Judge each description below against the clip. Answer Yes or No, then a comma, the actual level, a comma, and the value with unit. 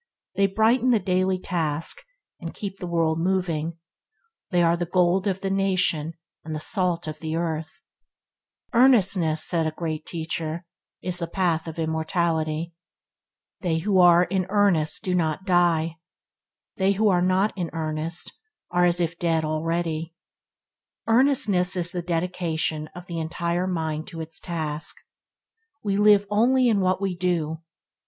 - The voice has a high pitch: No, medium, 175 Hz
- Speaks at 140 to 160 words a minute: Yes, average, 150 wpm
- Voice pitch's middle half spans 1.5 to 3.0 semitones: Yes, average, 2.7 semitones